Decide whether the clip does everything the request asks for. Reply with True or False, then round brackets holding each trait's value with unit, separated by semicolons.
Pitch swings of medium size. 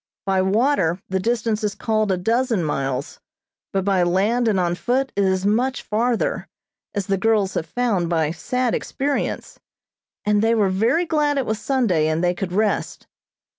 True (4.4 semitones)